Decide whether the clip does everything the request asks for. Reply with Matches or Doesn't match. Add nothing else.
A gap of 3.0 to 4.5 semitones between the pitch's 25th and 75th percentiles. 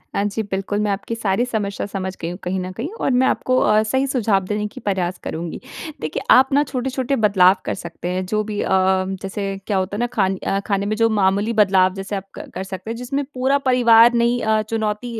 Matches